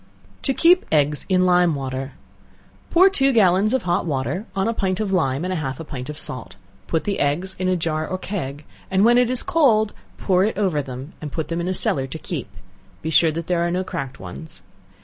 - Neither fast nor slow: No, fast, 225 wpm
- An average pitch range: Yes, average, 5.0 semitones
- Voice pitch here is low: No, medium, 175 Hz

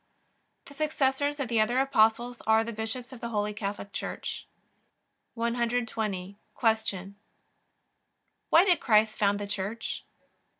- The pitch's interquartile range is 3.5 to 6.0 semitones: No, average, 2.9 semitones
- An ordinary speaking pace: No, slow, 125 wpm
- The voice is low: No, high, 225 Hz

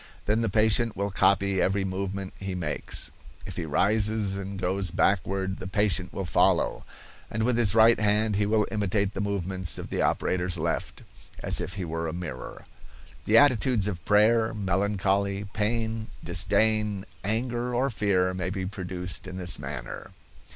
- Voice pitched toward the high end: No, low, 100 Hz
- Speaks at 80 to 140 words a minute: No, average, 160 wpm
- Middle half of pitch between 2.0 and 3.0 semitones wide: Yes, narrow, 2.6 semitones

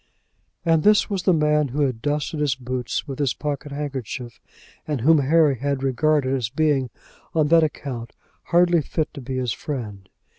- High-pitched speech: No, medium, 145 Hz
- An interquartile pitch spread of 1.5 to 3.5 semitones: Yes, average, 3.2 semitones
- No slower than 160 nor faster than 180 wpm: Yes, average, 175 wpm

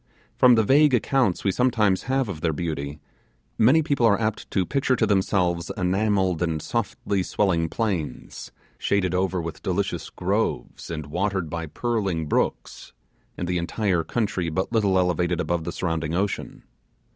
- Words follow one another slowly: No, average, 155 wpm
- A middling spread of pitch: Yes, average, 4.3 semitones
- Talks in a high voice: No, very low, 95 Hz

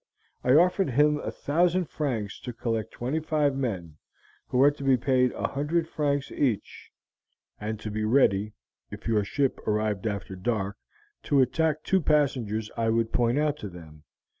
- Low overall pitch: Yes, low, 125 Hz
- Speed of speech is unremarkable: Yes, average, 165 wpm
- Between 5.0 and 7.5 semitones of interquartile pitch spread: Yes, wide, 5.4 semitones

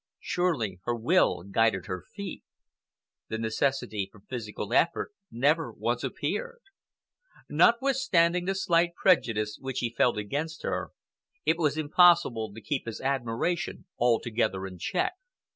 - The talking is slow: Yes, slow, 130 wpm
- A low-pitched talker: Yes, low, 130 Hz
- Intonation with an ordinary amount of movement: No, wide, 7.6 semitones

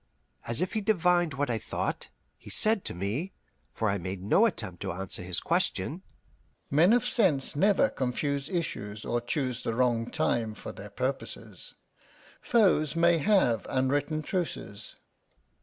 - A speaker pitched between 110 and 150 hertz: Yes, medium, 140 Hz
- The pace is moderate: Yes, average, 150 wpm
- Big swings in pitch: Yes, wide, 7.9 semitones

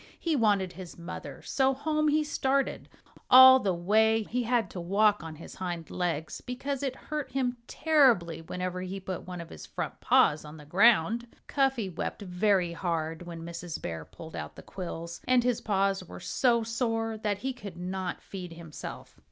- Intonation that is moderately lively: No, wide, 6.3 semitones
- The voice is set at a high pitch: Yes, high, 195 Hz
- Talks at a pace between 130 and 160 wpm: No, average, 180 wpm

